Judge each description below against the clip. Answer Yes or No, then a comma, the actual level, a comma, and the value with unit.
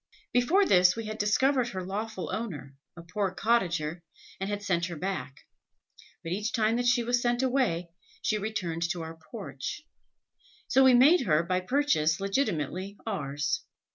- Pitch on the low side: No, high, 200 Hz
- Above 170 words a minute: No, average, 160 wpm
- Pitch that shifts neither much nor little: No, wide, 5.9 semitones